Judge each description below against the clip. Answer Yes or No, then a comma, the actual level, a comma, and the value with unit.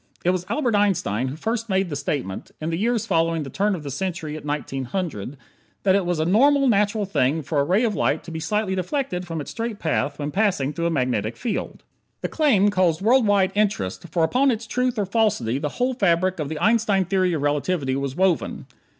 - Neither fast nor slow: No, fast, 220 wpm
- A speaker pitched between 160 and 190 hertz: Yes, medium, 185 Hz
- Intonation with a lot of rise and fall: Yes, wide, 5.9 semitones